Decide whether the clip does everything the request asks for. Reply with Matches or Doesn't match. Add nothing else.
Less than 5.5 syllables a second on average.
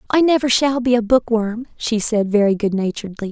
Doesn't match